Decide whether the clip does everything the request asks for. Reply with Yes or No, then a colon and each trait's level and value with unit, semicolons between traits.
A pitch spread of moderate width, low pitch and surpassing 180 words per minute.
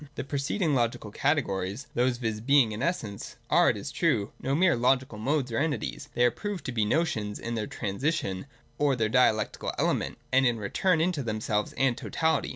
Yes: average, 5.0 semitones; low, 125 Hz; average, 200 wpm